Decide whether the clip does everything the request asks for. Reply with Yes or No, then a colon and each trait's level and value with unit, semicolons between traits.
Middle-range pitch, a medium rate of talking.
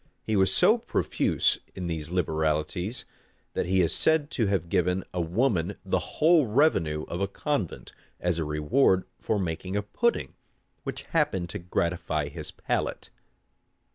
No: very low, 90 Hz; average, 150 wpm